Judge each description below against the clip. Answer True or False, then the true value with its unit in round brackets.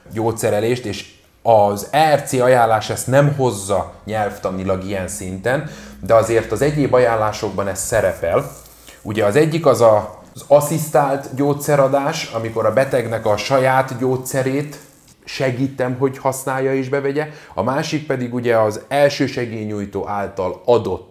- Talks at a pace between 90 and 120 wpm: False (130 wpm)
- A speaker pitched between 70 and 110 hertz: False (125 Hz)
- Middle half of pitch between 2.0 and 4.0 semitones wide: False (4.7 semitones)